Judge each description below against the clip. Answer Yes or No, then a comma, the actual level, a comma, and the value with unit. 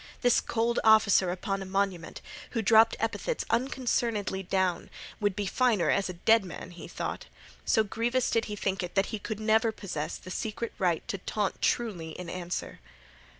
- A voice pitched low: No, high, 205 Hz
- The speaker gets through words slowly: No, average, 175 wpm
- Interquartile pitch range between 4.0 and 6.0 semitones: No, average, 3.4 semitones